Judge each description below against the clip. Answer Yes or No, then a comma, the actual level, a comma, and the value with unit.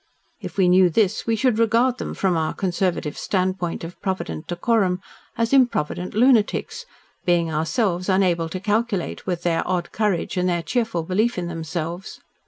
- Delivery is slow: No, average, 160 wpm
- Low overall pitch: No, medium, 185 Hz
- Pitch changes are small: No, average, 4.2 semitones